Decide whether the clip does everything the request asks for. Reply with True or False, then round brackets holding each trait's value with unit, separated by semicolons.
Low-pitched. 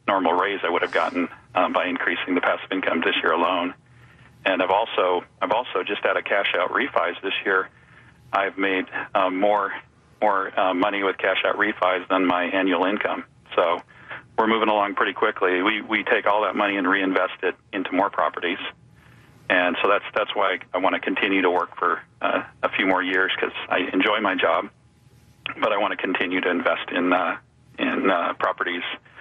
True (95 Hz)